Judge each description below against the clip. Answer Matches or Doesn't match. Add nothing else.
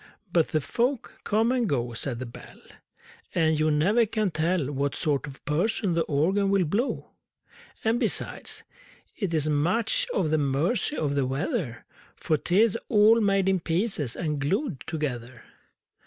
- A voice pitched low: Doesn't match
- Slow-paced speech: Doesn't match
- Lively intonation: Matches